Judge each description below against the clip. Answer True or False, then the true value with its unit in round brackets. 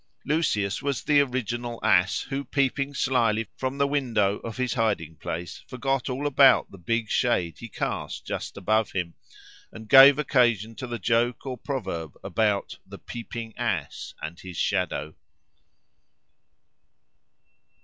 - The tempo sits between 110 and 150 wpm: True (140 wpm)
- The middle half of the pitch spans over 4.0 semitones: True (4.7 semitones)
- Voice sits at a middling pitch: False (115 Hz)